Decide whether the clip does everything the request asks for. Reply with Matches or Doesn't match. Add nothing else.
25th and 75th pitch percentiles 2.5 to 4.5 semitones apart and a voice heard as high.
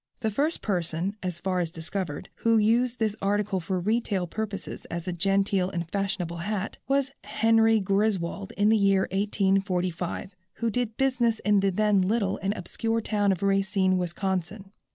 Matches